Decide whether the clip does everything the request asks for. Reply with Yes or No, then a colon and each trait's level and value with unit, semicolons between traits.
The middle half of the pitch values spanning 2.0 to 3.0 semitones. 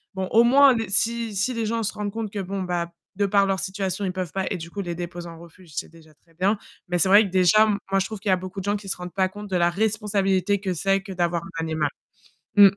Yes: narrow, 2.6 semitones